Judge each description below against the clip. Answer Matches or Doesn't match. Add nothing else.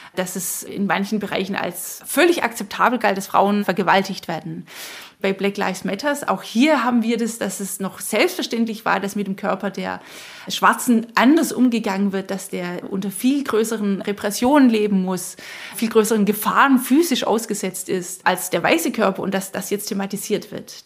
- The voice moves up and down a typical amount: Matches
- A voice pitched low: Doesn't match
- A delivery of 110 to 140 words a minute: Doesn't match